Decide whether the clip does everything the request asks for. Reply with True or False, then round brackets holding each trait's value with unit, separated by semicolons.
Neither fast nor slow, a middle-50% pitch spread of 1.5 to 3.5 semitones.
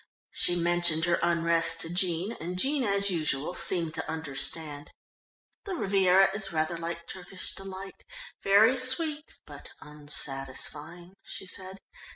False (130 wpm; 3.0 semitones)